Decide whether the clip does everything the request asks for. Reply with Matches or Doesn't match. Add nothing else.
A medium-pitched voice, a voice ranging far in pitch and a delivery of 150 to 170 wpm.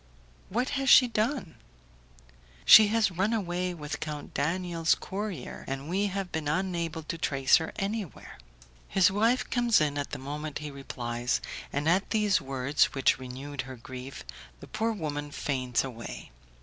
Matches